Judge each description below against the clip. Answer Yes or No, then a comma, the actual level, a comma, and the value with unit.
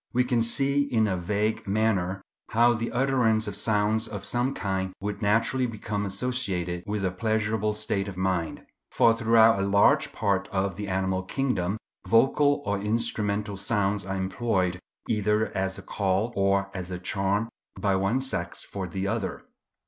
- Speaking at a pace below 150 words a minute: No, average, 165 wpm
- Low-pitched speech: Yes, low, 105 Hz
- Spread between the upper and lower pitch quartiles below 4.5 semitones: Yes, average, 2.9 semitones